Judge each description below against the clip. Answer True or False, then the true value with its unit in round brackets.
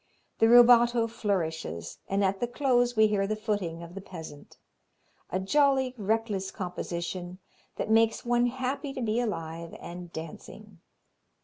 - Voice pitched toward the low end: False (210 Hz)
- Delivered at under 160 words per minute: True (140 wpm)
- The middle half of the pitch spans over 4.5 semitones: True (5.1 semitones)